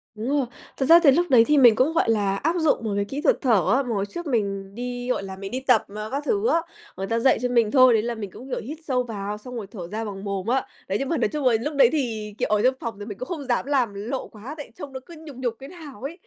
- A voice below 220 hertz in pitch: No, high, 245 Hz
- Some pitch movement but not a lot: Yes, average, 4.8 semitones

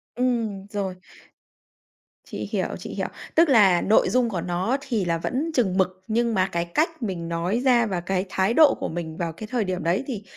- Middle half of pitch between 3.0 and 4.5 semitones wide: No, average, 5.0 semitones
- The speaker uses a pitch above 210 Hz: No, high, 195 Hz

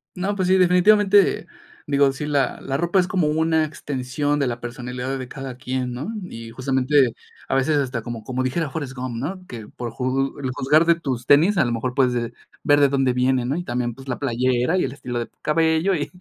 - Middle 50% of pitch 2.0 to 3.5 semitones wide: No, average, 4.1 semitones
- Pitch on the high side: No, low, 135 Hz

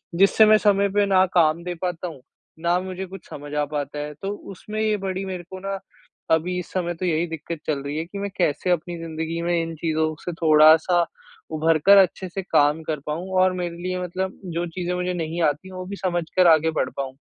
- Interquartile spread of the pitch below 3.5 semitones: Yes, average, 2.9 semitones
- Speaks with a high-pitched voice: No, medium, 175 Hz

